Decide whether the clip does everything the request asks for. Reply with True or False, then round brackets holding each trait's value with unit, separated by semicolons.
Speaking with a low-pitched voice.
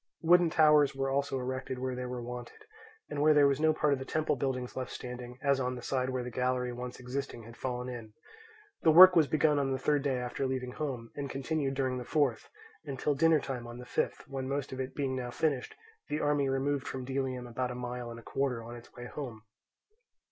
True (130 Hz)